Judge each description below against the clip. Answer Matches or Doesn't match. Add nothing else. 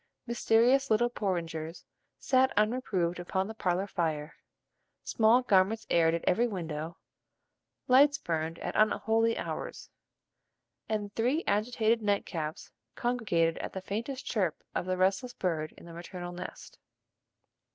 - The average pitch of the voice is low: Doesn't match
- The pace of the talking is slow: Matches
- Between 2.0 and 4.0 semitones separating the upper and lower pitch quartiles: Doesn't match